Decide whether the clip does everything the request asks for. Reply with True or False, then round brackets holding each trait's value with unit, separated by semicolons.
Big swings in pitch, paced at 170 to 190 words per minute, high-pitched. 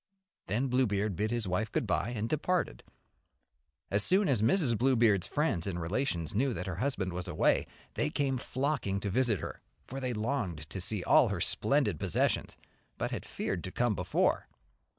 False (5.7 semitones; 175 wpm; 110 Hz)